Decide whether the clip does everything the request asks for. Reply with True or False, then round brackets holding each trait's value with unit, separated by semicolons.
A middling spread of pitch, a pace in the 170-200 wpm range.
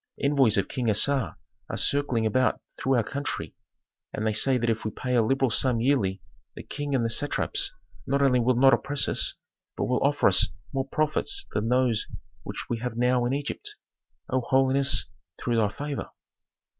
True (3.2 semitones; 180 wpm)